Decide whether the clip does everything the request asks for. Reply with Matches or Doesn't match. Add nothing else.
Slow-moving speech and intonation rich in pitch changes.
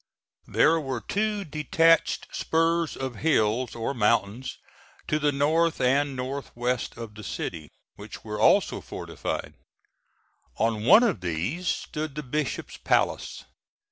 Matches